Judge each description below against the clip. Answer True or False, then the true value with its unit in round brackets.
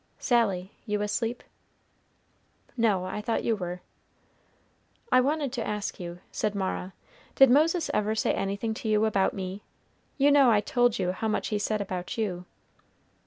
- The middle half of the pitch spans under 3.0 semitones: False (3.8 semitones)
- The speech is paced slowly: False (160 wpm)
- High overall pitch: True (210 Hz)